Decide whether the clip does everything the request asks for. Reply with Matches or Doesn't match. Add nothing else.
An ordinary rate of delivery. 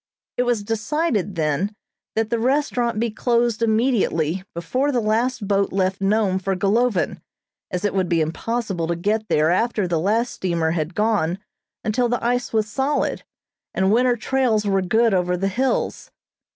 Matches